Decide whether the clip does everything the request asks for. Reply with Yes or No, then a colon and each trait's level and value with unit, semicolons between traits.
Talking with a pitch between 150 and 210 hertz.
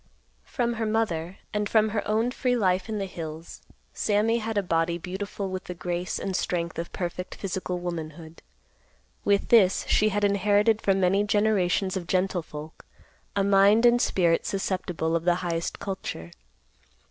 Yes: high, 190 Hz